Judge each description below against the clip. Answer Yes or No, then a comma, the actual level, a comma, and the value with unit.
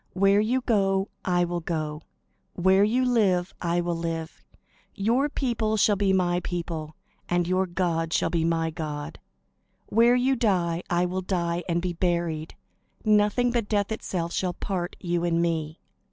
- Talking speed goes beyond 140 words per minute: Yes, average, 160 wpm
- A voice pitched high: No, medium, 180 Hz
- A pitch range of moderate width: Yes, average, 3.3 semitones